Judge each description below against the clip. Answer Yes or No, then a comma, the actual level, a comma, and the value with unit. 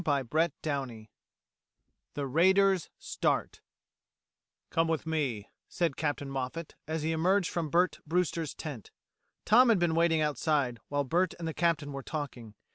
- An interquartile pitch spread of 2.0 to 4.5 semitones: Yes, average, 3.4 semitones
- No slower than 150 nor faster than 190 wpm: No, average, 140 wpm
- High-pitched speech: No, medium, 160 Hz